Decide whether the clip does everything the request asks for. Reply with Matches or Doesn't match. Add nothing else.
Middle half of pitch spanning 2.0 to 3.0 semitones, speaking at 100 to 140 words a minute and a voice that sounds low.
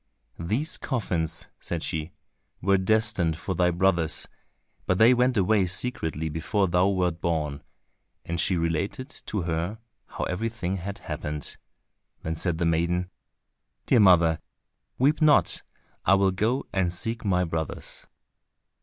Doesn't match